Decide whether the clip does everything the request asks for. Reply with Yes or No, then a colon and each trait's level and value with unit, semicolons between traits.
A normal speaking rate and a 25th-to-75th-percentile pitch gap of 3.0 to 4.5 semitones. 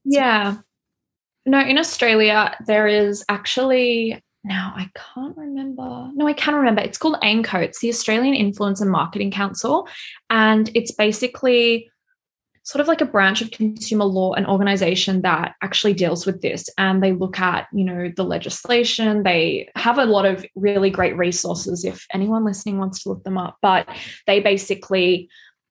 Yes: average, 165 wpm; average, 3.7 semitones